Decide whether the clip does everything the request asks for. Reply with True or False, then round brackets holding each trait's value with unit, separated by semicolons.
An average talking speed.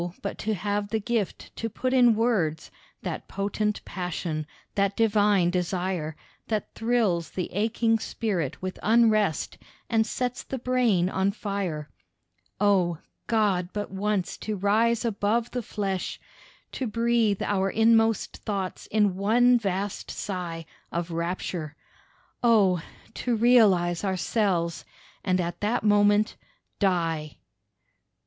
False (120 wpm)